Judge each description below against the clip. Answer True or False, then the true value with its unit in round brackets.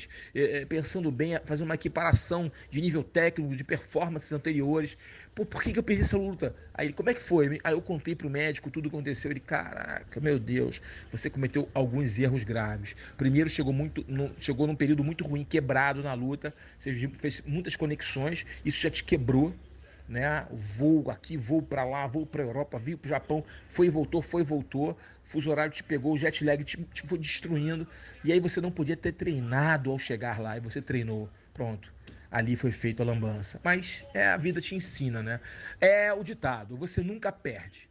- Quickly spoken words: True (190 wpm)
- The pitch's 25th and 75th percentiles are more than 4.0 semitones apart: False (3.6 semitones)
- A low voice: False (150 Hz)